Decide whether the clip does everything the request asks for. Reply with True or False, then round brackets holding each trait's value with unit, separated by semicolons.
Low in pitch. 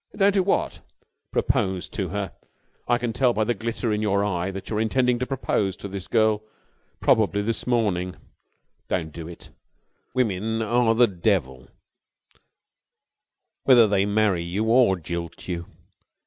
True (105 Hz)